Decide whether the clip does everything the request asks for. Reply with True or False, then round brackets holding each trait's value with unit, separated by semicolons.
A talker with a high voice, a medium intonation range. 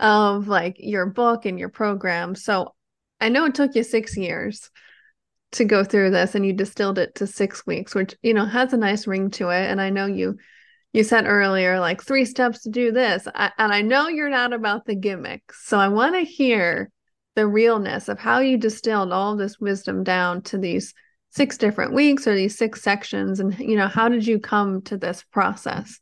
True (210 Hz; 3.5 semitones)